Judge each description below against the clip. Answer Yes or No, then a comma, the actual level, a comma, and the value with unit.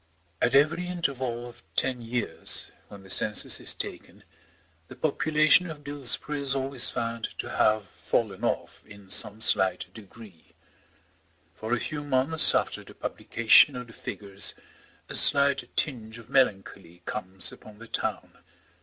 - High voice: No, low, 120 Hz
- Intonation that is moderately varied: Yes, average, 4.8 semitones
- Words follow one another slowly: No, average, 145 wpm